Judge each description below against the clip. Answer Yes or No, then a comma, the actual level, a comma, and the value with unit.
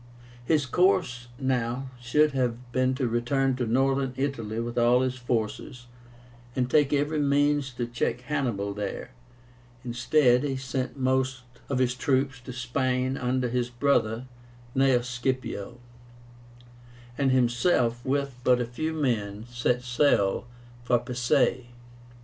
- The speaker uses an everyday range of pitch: No, narrow, 1.9 semitones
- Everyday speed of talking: No, slow, 130 wpm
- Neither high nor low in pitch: No, low, 125 Hz